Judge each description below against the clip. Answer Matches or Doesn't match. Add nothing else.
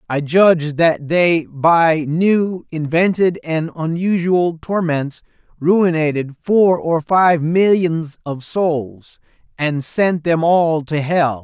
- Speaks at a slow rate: Matches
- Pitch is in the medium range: Matches